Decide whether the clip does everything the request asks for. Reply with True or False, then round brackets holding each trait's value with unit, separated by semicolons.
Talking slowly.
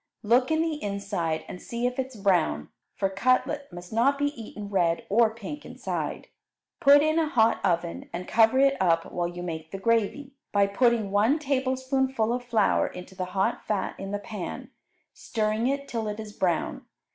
False (185 wpm)